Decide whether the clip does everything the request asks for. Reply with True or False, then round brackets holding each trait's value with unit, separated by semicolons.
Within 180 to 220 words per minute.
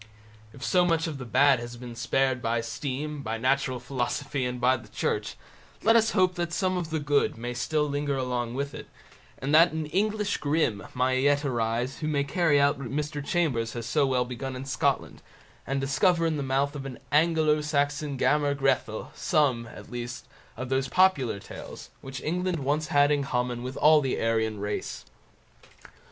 True (190 wpm)